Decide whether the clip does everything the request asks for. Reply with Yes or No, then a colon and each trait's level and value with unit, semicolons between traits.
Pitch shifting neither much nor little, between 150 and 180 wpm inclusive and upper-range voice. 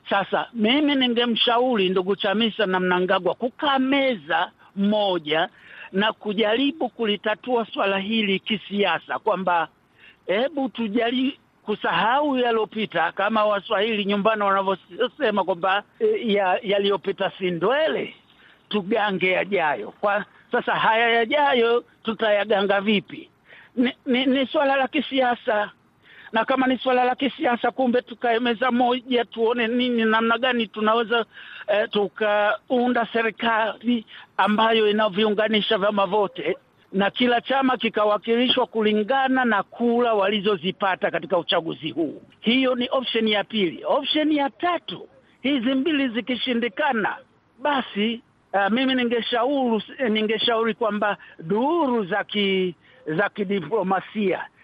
No: average, 3.6 semitones; slow, 100 wpm; high, 225 Hz